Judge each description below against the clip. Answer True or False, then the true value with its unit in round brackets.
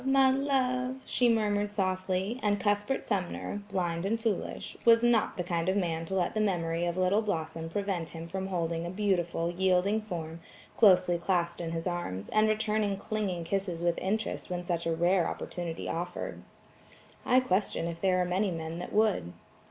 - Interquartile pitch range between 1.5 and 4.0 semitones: True (3.6 semitones)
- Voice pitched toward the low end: False (185 Hz)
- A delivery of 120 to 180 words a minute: True (175 wpm)